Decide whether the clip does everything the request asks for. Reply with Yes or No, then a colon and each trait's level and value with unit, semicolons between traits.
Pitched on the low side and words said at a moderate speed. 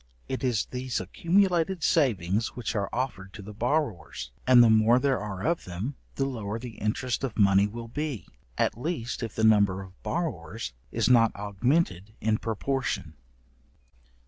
Yes: low, 115 Hz; average, 160 wpm